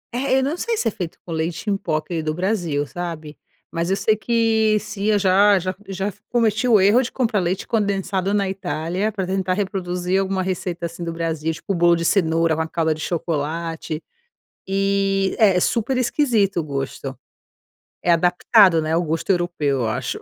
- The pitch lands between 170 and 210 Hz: Yes, medium, 185 Hz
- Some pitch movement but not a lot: Yes, average, 3.6 semitones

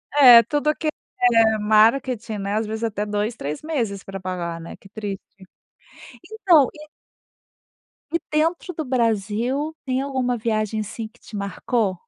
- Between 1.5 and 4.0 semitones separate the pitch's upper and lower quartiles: No, average, 4.7 semitones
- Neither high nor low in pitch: No, high, 225 Hz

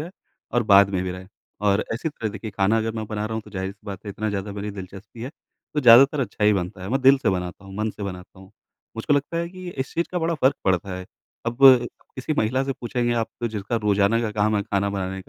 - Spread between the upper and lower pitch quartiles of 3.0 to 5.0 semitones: Yes, average, 3.6 semitones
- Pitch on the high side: No, low, 105 Hz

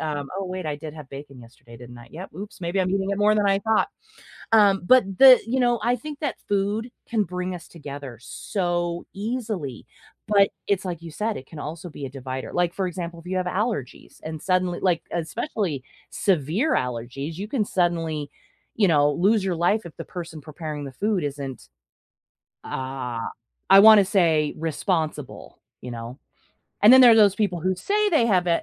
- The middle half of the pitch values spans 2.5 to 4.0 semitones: No, wide, 5.5 semitones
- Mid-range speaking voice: Yes, medium, 175 Hz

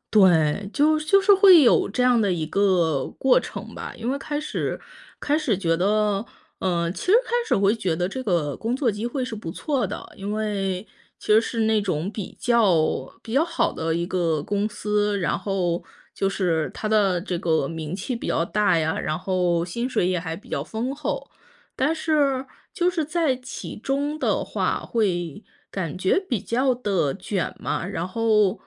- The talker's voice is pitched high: Yes, high, 205 Hz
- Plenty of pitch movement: Yes, wide, 6.1 semitones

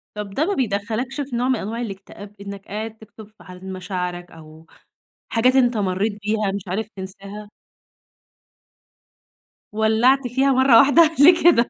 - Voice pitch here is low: No, high, 215 Hz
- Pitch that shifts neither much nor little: Yes, average, 4.3 semitones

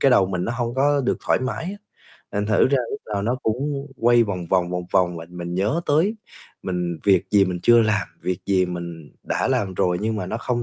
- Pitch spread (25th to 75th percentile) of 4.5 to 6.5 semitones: Yes, average, 5.0 semitones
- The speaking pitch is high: No, low, 100 Hz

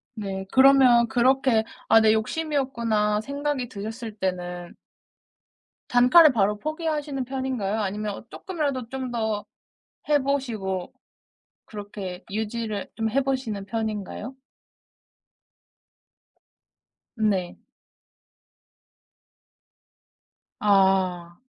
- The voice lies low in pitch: No, high, 225 Hz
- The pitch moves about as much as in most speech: Yes, average, 4.6 semitones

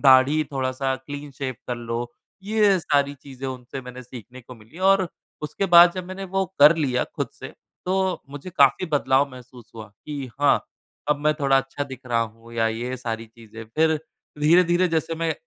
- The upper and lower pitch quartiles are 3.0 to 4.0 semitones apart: No, average, 4.7 semitones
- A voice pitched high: No, medium, 140 Hz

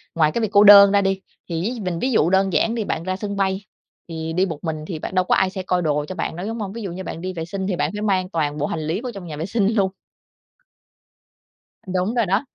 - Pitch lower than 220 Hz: Yes, high, 190 Hz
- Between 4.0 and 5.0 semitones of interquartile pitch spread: No, average, 3.3 semitones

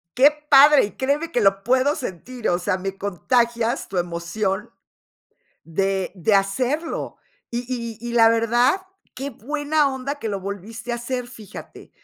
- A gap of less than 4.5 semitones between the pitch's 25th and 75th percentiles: No, average, 4.9 semitones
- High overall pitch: Yes, high, 235 Hz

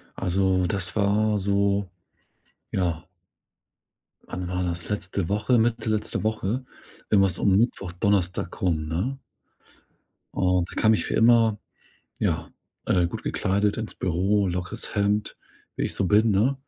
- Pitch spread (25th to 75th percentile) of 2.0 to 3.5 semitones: Yes, average, 2.9 semitones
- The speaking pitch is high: No, low, 100 Hz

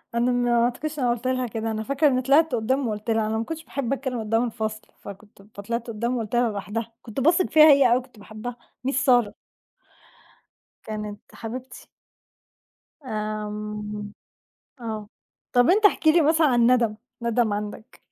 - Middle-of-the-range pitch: No, high, 235 Hz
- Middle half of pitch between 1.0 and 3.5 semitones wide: Yes, average, 3.2 semitones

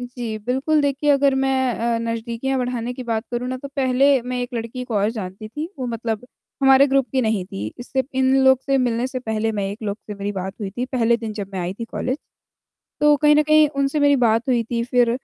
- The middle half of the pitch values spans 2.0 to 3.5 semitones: Yes, average, 3.1 semitones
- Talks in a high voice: Yes, high, 245 Hz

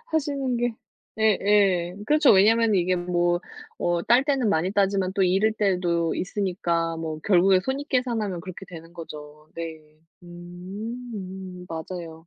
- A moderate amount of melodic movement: Yes, average, 4.1 semitones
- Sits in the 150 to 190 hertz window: Yes, medium, 185 Hz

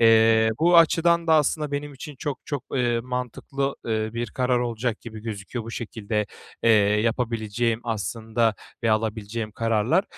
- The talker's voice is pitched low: Yes, low, 115 Hz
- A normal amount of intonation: Yes, average, 3.2 semitones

